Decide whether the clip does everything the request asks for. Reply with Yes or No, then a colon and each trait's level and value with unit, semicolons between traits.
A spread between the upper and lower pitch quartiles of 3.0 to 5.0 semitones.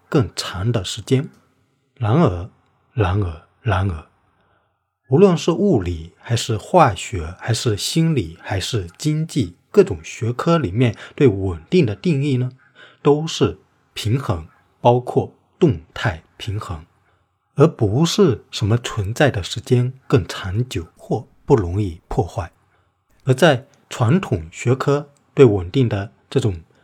No: wide, 5.6 semitones